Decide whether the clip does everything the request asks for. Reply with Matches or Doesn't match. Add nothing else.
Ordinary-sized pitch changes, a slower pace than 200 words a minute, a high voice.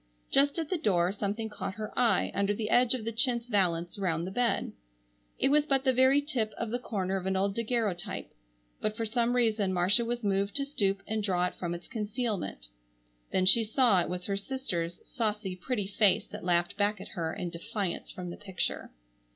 Doesn't match